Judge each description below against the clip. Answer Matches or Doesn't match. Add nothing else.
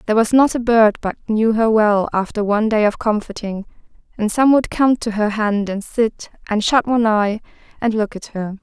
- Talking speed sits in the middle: Doesn't match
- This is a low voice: Doesn't match